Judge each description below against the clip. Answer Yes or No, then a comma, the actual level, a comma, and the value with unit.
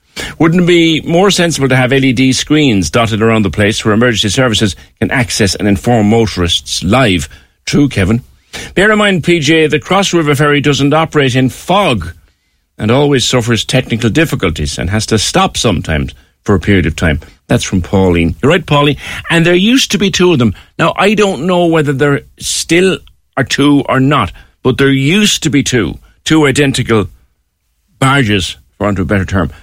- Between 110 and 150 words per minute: No, average, 185 wpm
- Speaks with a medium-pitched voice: No, low, 125 Hz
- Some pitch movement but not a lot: No, wide, 7.8 semitones